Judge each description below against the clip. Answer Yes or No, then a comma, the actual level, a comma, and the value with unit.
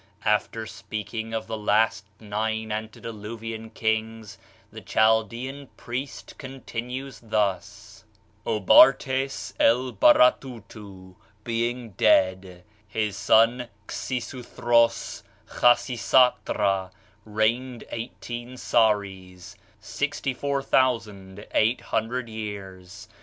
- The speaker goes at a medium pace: No, slow, 65 wpm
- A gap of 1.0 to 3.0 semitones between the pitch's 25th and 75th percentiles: Yes, average, 2.7 semitones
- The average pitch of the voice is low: Yes, low, 110 Hz